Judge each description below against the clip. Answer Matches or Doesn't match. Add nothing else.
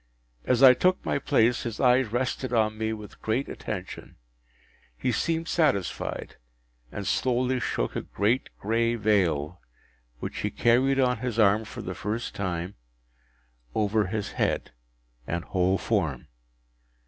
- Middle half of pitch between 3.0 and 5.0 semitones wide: Matches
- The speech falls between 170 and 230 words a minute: Doesn't match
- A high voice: Doesn't match